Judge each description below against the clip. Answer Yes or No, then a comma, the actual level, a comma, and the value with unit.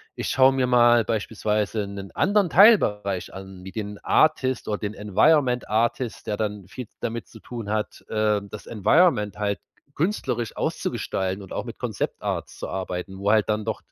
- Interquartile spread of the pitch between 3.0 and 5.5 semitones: Yes, average, 3.3 semitones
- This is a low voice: Yes, low, 110 Hz